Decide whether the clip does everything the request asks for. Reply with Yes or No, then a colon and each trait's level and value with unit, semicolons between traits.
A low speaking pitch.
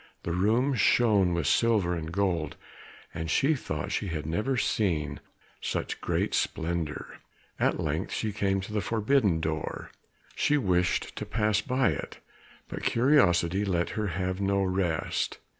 Yes: very low, 95 Hz